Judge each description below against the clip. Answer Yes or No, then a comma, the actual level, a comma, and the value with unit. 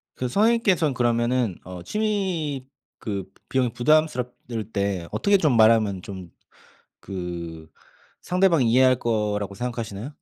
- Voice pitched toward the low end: Yes, low, 120 Hz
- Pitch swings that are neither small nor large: No, wide, 7.2 semitones